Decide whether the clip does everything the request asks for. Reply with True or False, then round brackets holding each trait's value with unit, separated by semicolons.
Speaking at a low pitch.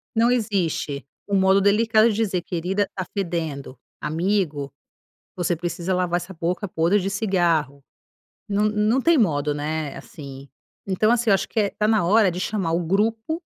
False (190 Hz)